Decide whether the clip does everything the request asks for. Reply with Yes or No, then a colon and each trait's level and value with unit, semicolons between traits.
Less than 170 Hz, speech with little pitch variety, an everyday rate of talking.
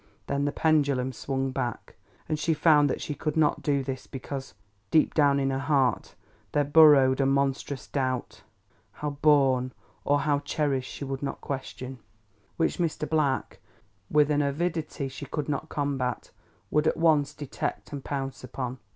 Yes: medium, 140 Hz; narrow, 1.9 semitones; average, 160 wpm